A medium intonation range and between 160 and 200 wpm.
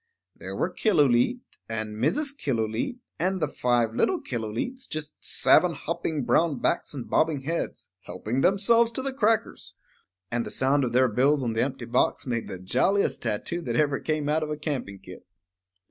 No: wide, 6.2 semitones; average, 175 wpm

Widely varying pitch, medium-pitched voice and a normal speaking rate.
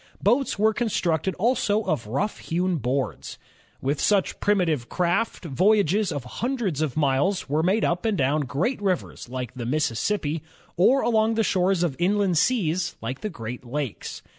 Yes: wide, 6.6 semitones; medium, 175 Hz; average, 160 wpm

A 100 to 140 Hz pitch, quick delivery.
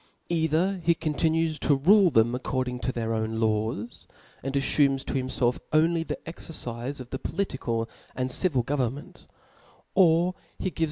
No: low, 135 Hz; average, 145 wpm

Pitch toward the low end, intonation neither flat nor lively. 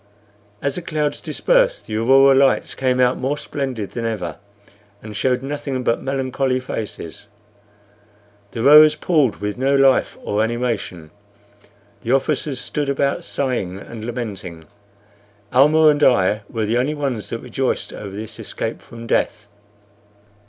Yes: low, 125 Hz; average, 4.0 semitones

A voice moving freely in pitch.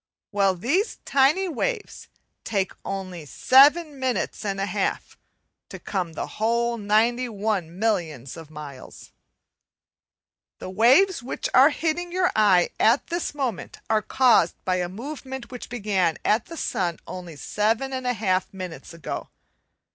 Yes: wide, 6.2 semitones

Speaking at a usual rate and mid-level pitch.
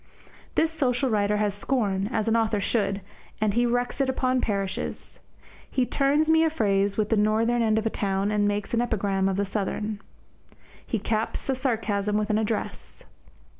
No: average, 180 wpm; high, 215 Hz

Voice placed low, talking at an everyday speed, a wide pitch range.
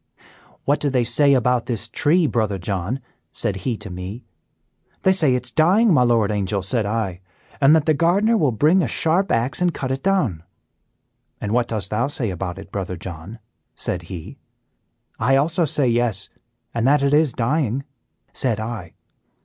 Yes: low, 120 Hz; average, 180 wpm; wide, 6.4 semitones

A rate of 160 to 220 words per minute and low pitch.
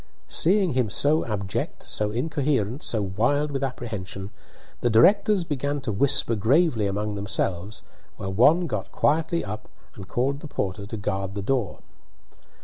No: average, 145 wpm; low, 115 Hz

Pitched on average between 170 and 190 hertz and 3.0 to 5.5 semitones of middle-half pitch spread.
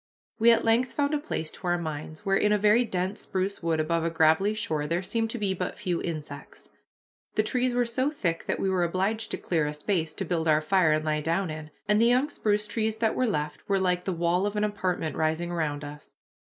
Yes: medium, 185 Hz; average, 5.0 semitones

